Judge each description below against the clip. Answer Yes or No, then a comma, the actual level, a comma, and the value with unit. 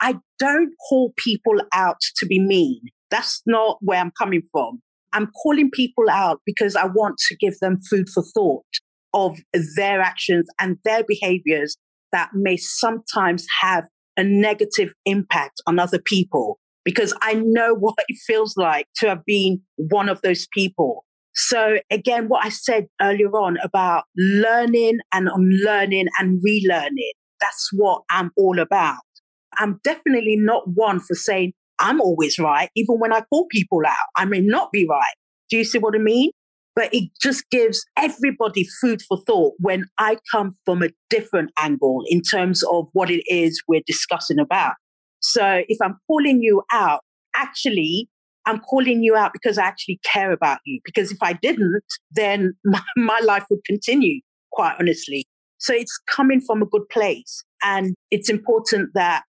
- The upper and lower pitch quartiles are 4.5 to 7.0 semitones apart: No, average, 3.9 semitones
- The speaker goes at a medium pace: Yes, average, 165 wpm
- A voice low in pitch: No, high, 210 Hz